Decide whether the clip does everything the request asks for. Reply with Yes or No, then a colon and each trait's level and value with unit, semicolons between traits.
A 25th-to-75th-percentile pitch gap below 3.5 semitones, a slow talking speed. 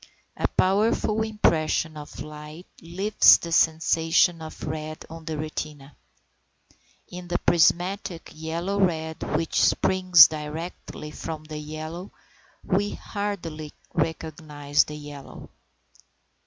Yes: average, 2.7 semitones; slow, 105 wpm